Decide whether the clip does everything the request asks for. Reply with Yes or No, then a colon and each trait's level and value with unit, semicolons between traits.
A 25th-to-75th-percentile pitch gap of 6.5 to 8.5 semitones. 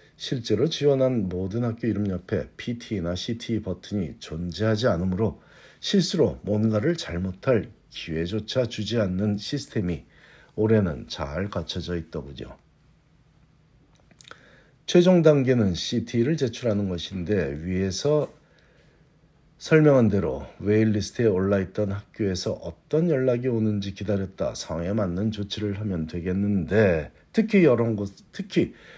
No: average, 5.2 semitones